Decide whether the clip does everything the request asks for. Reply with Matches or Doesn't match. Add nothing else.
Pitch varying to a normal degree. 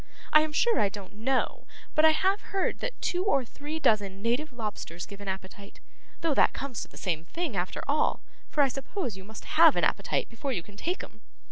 Doesn't match